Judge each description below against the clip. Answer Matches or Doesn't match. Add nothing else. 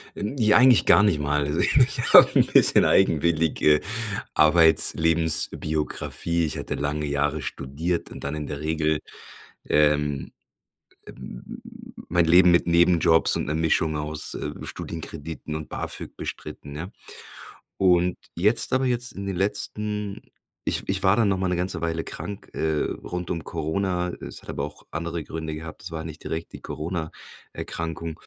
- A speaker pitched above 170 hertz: Doesn't match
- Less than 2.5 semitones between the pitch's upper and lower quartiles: Doesn't match